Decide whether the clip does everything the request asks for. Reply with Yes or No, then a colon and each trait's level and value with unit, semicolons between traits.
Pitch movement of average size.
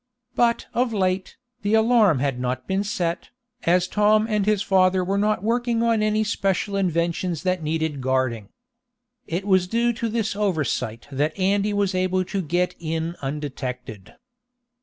Yes: average, 4.8 semitones